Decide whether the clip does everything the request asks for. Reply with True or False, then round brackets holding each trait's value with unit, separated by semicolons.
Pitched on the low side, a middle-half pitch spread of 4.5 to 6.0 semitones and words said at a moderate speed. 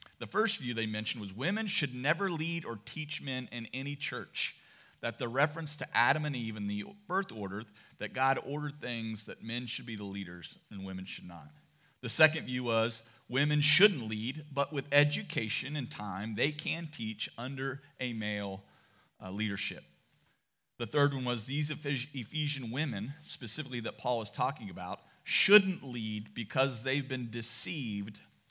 True (125 Hz; 5.0 semitones; 165 wpm)